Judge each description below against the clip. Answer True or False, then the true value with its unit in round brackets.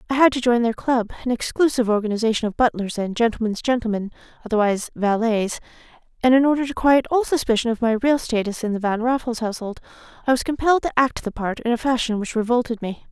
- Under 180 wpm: False (190 wpm)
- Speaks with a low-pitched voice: False (235 Hz)